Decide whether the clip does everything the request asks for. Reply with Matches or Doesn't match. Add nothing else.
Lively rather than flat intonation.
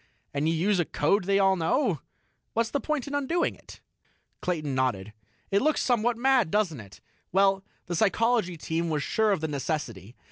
Matches